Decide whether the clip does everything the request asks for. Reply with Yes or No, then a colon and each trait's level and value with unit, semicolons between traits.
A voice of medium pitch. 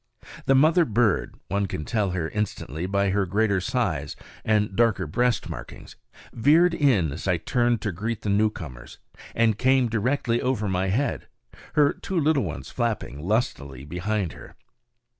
No: low, 105 Hz